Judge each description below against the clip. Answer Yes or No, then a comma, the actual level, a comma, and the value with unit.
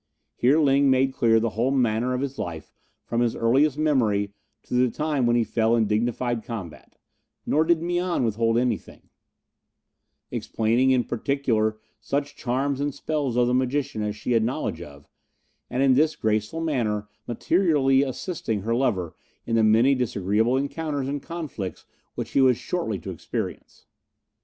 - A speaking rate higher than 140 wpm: Yes, average, 160 wpm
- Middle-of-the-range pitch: No, low, 125 Hz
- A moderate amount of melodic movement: Yes, average, 4.0 semitones